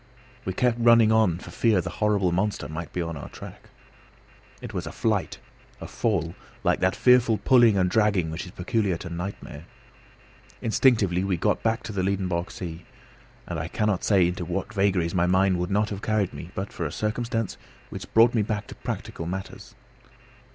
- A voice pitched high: No, very low, 95 Hz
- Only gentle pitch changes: No, average, 3.7 semitones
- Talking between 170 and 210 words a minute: Yes, average, 185 wpm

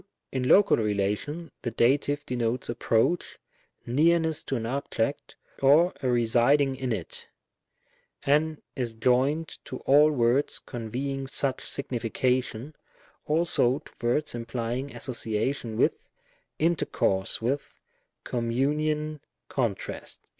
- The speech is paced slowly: Yes, slow, 105 wpm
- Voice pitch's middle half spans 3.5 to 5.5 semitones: Yes, average, 3.8 semitones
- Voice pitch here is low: Yes, low, 130 Hz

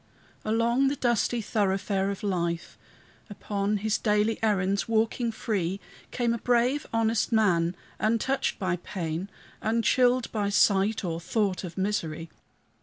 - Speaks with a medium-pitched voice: No, high, 210 Hz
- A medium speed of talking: No, slow, 125 wpm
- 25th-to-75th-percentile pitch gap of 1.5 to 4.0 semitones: Yes, average, 3.2 semitones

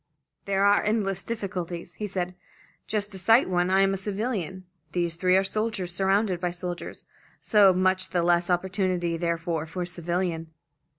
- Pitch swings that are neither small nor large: No, narrow, 2.1 semitones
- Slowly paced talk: No, average, 165 wpm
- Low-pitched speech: No, medium, 185 Hz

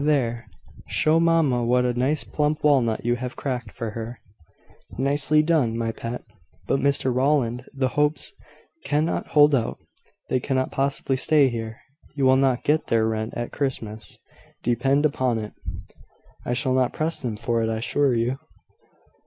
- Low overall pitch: Yes, low, 130 Hz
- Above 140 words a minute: Yes, average, 160 wpm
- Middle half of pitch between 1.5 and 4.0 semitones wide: Yes, average, 3.6 semitones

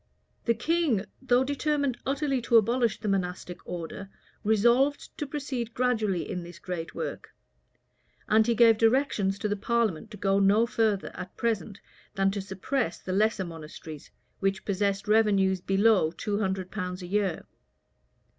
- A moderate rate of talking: Yes, average, 150 wpm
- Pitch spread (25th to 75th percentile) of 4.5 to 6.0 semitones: No, average, 3.7 semitones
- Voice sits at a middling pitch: No, high, 210 Hz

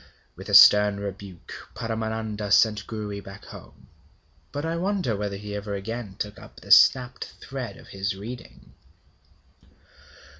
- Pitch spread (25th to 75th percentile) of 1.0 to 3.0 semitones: Yes, narrow, 2.6 semitones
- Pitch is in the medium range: No, low, 105 Hz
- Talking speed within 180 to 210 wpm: No, average, 140 wpm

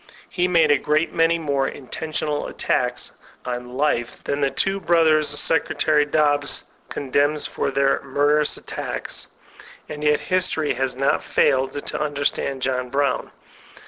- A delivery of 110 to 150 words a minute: Yes, average, 145 wpm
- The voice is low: No, medium, 145 Hz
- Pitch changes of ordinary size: No, narrow, 2.1 semitones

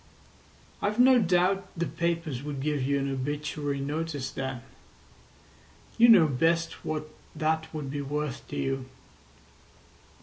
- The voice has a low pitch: No, medium, 150 Hz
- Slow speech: Yes, slow, 130 wpm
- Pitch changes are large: No, average, 3.1 semitones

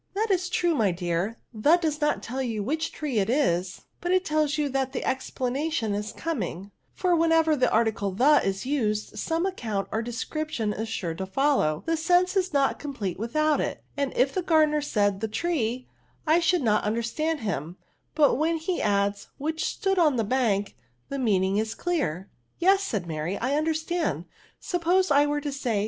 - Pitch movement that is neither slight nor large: No, wide, 7.2 semitones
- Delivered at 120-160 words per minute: No, average, 195 wpm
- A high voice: Yes, very high, 270 Hz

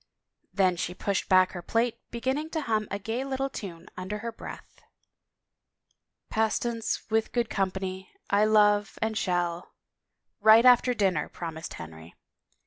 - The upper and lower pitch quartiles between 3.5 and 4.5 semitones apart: Yes, average, 3.8 semitones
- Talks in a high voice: Yes, high, 210 Hz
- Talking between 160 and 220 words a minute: No, average, 145 wpm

